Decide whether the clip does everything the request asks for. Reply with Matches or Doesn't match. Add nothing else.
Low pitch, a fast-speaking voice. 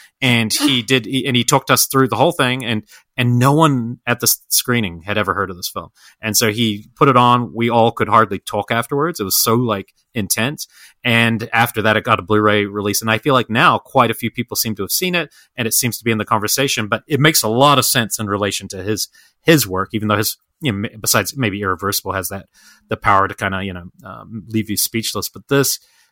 Matches